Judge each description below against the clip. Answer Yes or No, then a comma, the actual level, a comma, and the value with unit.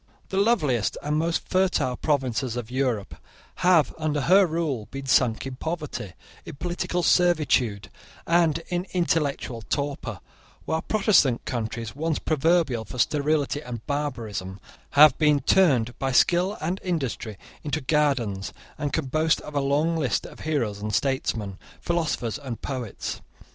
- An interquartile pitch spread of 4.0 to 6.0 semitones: Yes, average, 5.0 semitones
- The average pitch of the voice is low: No, medium, 145 Hz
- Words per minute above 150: No, average, 140 wpm